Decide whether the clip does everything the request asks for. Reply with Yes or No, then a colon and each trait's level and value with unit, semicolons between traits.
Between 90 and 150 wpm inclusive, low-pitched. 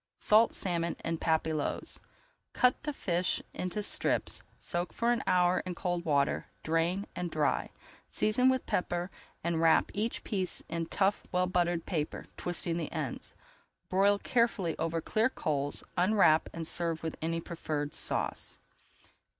No: average, 140 wpm; medium, 175 Hz